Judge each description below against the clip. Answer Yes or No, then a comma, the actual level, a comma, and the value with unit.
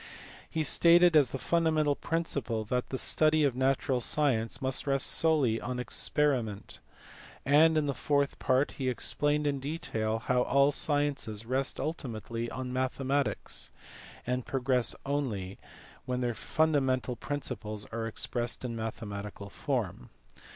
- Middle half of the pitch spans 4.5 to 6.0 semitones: No, average, 3.7 semitones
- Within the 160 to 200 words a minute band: No, slow, 135 wpm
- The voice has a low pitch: Yes, low, 130 Hz